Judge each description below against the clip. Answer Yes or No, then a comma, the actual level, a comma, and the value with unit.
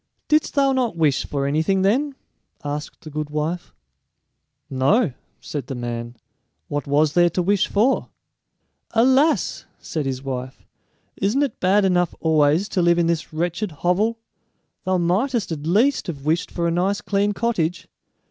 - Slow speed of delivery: No, average, 155 wpm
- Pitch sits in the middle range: Yes, medium, 175 Hz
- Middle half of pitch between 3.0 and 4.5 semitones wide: No, wide, 5.5 semitones